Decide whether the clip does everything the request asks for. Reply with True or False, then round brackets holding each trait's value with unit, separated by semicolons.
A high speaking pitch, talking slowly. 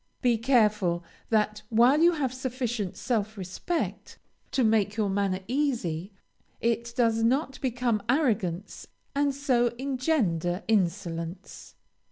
True (225 Hz; 115 wpm)